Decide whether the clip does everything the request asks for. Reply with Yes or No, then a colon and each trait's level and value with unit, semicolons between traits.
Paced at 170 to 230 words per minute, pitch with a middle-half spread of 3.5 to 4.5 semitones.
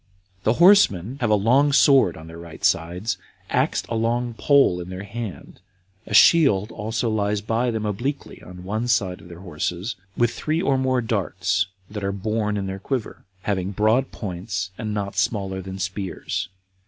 Yes: average, 175 wpm; average, 4.0 semitones